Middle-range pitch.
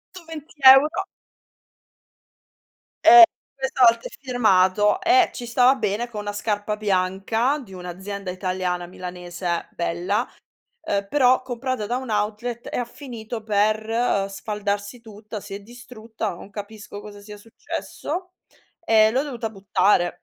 No: high, 215 Hz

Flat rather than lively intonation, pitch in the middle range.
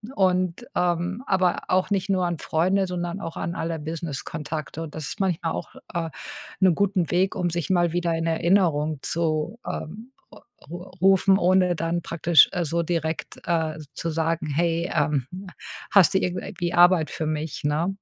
Yes: narrow, 2.3 semitones; medium, 170 Hz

